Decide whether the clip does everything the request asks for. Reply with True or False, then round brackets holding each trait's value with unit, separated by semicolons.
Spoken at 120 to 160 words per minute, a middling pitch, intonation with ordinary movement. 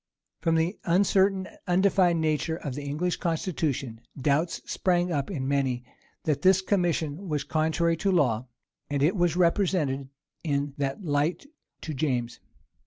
True (145 wpm; 160 Hz; 4.1 semitones)